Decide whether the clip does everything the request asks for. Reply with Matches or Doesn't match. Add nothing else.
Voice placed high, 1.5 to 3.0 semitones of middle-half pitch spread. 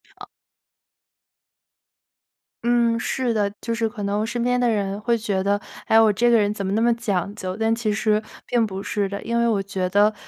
Matches